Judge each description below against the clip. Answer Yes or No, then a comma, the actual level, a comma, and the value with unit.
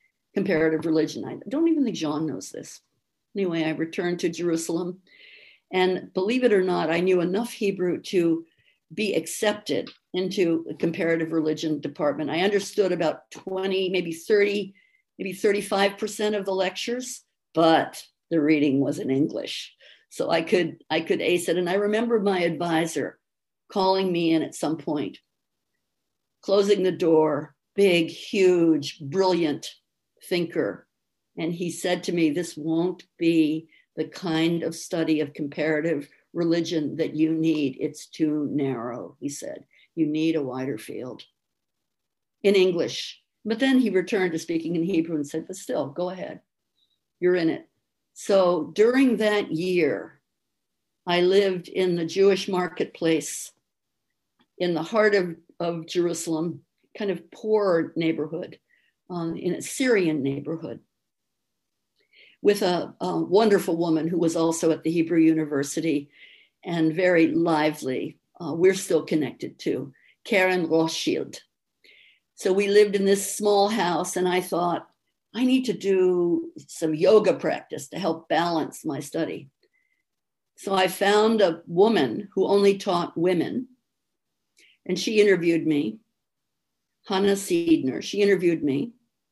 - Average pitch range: Yes, average, 3.7 semitones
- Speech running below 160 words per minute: Yes, average, 140 wpm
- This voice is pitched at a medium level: Yes, medium, 175 Hz